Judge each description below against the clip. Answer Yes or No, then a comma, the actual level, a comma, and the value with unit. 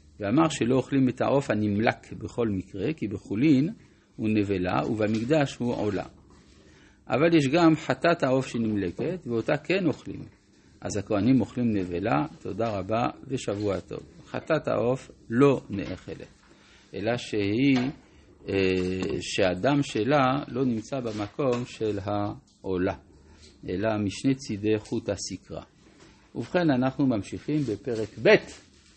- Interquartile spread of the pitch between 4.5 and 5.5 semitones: Yes, average, 5.1 semitones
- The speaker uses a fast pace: No, average, 115 wpm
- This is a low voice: Yes, low, 110 Hz